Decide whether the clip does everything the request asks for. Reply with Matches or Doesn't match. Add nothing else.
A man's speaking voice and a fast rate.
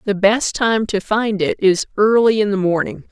Doesn't match